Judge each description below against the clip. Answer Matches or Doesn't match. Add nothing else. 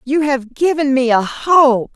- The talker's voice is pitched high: Matches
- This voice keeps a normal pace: Matches